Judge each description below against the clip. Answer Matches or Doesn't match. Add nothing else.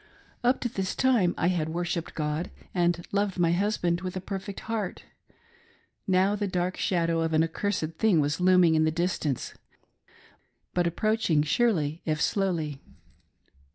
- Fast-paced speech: Doesn't match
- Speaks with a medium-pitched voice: Matches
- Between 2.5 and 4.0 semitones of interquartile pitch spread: Matches